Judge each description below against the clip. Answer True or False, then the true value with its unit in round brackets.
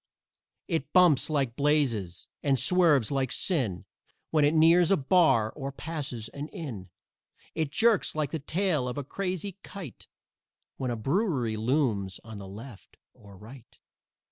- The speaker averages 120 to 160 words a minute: True (145 wpm)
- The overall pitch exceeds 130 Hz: True (140 Hz)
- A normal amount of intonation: False (5.9 semitones)